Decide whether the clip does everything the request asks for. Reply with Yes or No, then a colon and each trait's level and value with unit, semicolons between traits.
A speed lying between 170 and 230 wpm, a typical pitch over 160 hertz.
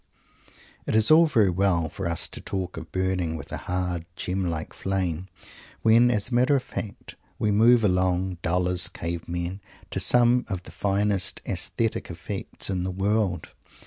No: average, 175 wpm; very low, 95 Hz